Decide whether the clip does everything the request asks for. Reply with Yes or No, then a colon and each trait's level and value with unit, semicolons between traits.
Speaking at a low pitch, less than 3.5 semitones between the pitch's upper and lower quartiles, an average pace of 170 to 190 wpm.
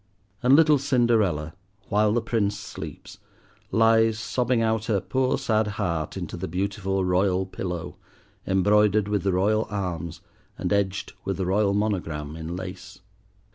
No: low, 100 Hz; average, 3.1 semitones; average, 140 wpm